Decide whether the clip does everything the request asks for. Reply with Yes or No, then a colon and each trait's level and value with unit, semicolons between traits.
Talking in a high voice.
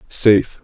No: low, 105 Hz